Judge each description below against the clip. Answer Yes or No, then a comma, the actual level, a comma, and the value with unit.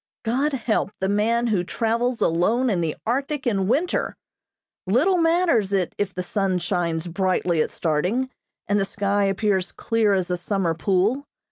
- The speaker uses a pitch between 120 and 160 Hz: No, high, 205 Hz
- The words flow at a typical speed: Yes, average, 160 wpm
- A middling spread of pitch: Yes, average, 4.8 semitones